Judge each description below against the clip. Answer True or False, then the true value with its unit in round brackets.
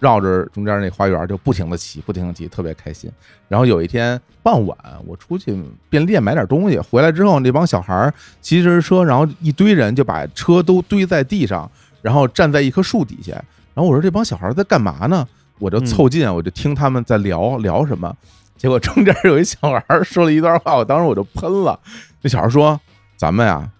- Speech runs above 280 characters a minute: True (310 characters per minute)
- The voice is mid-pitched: False (130 Hz)